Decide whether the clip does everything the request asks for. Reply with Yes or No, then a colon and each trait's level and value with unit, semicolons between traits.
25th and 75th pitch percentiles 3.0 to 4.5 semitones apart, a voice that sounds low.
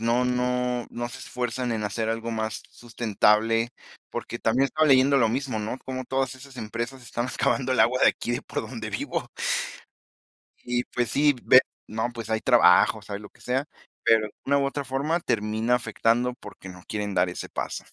No: narrow, 2.6 semitones; low, 120 Hz